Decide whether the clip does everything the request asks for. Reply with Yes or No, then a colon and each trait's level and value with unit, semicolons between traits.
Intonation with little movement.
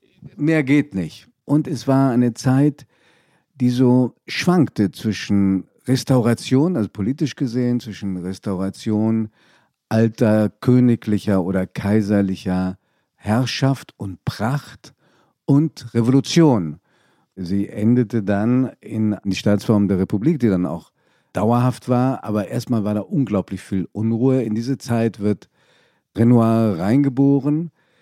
No: average, 4.4 semitones